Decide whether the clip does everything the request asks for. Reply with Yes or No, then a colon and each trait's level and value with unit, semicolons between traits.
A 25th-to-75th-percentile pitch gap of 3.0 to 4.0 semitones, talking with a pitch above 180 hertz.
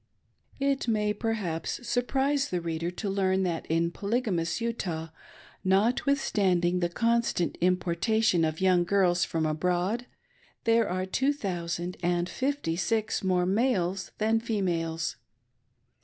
No: average, 4.7 semitones; high, 190 Hz